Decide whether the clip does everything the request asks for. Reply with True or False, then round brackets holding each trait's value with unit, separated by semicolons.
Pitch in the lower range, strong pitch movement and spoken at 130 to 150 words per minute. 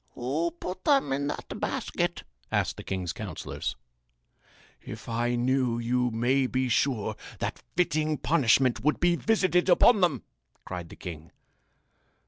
True (130 Hz; 5.7 semitones; 135 wpm)